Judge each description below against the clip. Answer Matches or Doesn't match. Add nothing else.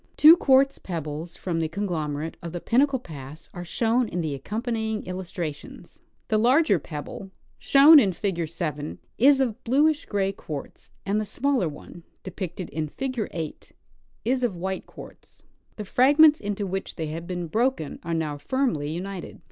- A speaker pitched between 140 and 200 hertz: Matches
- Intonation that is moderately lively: Doesn't match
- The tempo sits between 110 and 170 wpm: Matches